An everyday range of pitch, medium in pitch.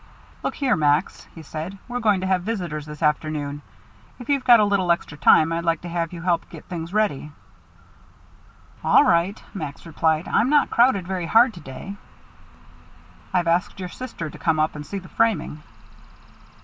Yes: average, 4.6 semitones; medium, 175 Hz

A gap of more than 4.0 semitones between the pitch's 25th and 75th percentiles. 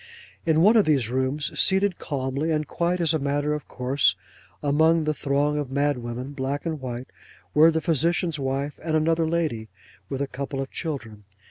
No: average, 3.1 semitones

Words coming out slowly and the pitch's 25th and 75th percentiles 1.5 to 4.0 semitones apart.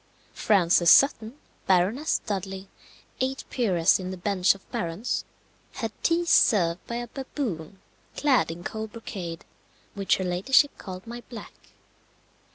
No: slow, 130 wpm; average, 4.9 semitones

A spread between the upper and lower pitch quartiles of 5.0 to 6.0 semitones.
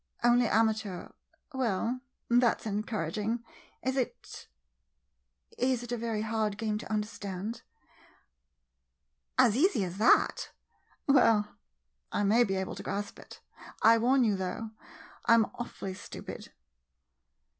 No: average, 3.2 semitones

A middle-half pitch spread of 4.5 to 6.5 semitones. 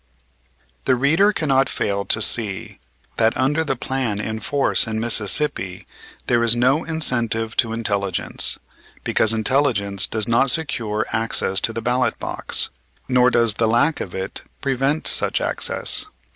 No: average, 3.6 semitones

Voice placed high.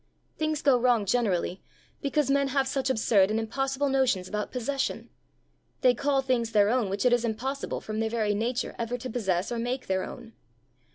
Yes: high, 240 Hz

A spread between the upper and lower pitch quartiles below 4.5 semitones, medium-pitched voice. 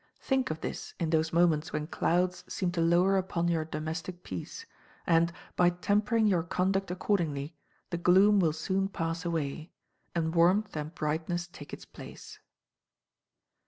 Yes: narrow, 2.5 semitones; medium, 175 Hz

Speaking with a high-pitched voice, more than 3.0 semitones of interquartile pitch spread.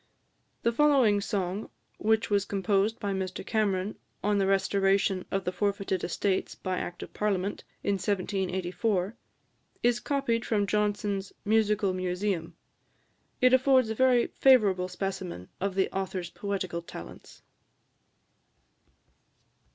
No: high, 200 Hz; narrow, 2.4 semitones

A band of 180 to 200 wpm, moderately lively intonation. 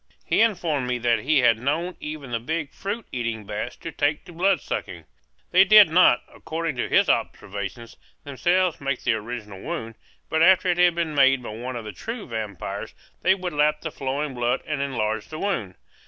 No: average, 190 wpm; wide, 6.3 semitones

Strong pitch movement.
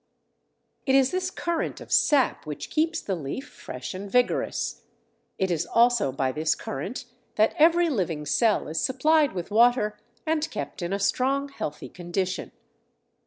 Yes: wide, 8.3 semitones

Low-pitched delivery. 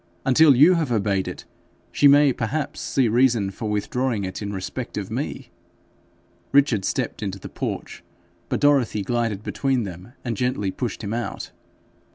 Yes: low, 120 Hz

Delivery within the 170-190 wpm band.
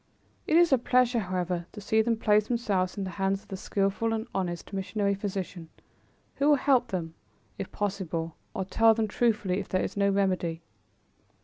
Yes: average, 185 wpm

